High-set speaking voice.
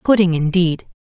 No: medium, 175 Hz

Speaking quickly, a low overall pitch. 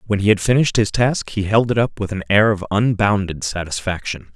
Yes: fast, 220 wpm; low, 100 Hz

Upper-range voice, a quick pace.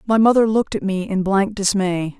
Yes: high, 200 Hz; fast, 220 wpm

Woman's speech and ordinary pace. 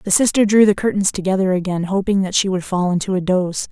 No: female; fast, 240 wpm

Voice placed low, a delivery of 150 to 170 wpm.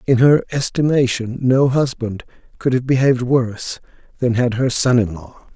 Yes: low, 125 Hz; average, 160 wpm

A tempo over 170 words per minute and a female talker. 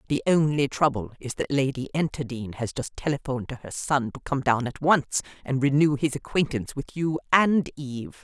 Yes: average, 190 wpm; female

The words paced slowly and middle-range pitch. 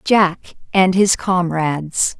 Yes: slow, 110 wpm; medium, 180 Hz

